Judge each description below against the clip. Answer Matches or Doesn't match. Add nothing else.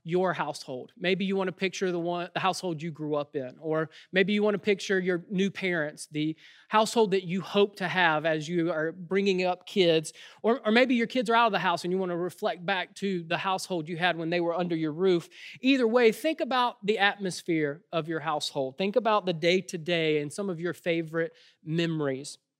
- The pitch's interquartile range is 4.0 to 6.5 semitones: Doesn't match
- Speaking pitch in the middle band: Matches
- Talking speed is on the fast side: Matches